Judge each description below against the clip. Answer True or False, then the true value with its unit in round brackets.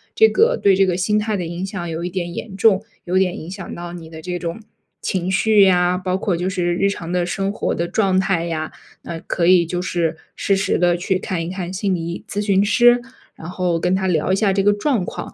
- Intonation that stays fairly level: True (2.2 semitones)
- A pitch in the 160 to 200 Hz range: True (185 Hz)